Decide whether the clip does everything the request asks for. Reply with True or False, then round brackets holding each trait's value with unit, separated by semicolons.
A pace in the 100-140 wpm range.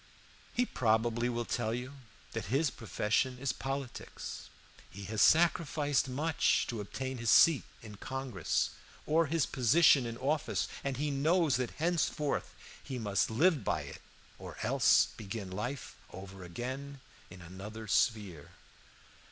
True (135 wpm)